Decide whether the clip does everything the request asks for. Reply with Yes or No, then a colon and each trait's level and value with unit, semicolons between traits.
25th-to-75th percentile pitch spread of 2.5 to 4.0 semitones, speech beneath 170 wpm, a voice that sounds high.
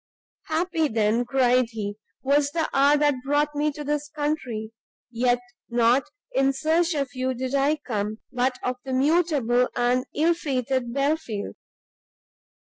Yes: average, 3.4 semitones; average, 140 wpm; very high, 270 Hz